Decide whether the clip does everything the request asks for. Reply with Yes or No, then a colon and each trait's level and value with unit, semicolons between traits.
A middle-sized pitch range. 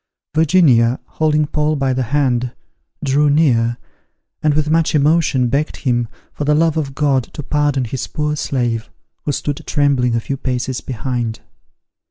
Yes: average, 3.3 semitones